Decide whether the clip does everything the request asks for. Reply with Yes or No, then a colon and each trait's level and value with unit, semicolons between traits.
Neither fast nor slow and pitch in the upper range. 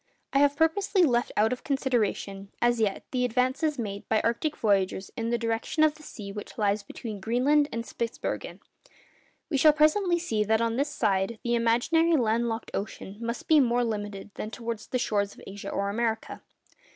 Yes: average, 185 wpm; high, 235 Hz